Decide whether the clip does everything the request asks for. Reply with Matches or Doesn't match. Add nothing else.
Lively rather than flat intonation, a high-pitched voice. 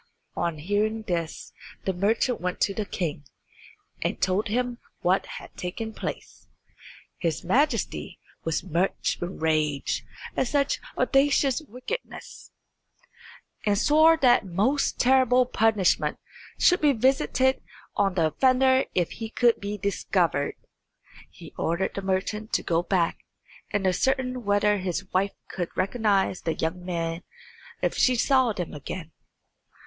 Matches